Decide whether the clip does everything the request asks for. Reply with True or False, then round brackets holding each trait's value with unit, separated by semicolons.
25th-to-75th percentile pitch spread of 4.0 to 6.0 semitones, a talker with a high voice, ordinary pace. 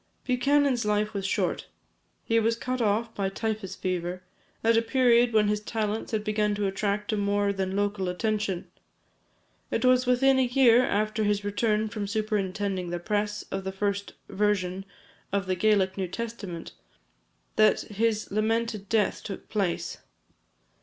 False (2.4 semitones; 210 Hz; 155 wpm)